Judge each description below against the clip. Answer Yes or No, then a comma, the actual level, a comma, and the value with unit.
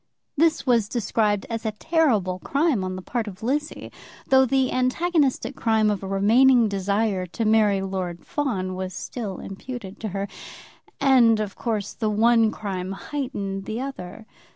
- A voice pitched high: Yes, high, 220 Hz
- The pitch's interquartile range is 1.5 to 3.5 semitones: No, average, 4.6 semitones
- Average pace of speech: Yes, average, 155 wpm